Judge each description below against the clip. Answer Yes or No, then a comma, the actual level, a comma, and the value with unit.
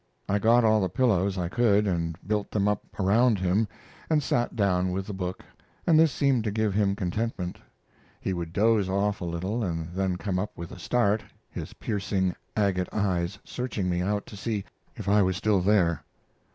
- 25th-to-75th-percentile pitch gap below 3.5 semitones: Yes, average, 2.9 semitones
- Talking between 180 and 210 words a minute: Yes, average, 190 wpm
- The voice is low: Yes, low, 100 Hz